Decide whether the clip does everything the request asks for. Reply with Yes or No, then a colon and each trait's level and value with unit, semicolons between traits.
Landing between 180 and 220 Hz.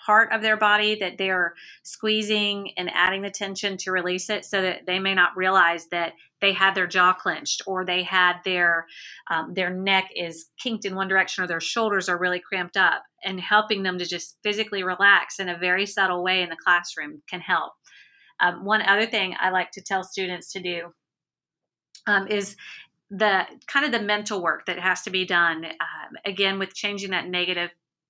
Yes: medium, 185 Hz